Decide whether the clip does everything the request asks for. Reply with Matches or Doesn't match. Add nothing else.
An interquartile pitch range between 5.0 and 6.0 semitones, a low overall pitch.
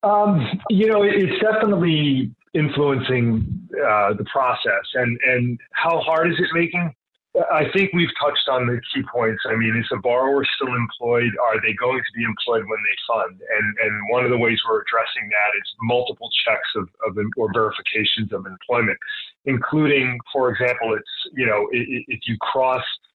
Matches